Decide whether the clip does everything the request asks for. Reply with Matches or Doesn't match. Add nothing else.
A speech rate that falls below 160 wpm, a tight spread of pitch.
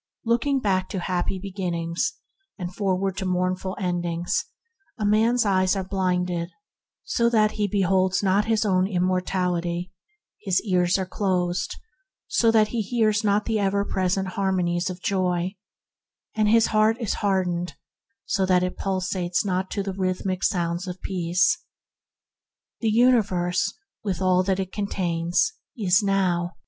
Matches